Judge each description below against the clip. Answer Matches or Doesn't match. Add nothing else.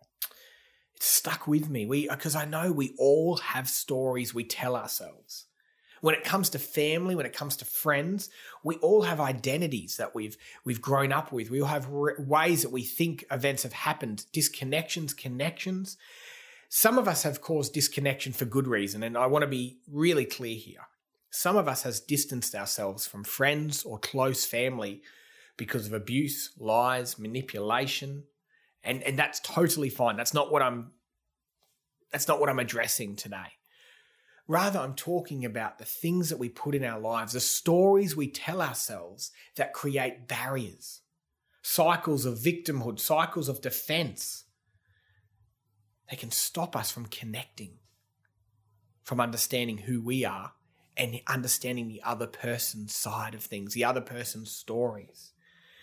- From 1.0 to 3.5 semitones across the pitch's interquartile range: Doesn't match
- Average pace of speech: Matches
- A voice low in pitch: Matches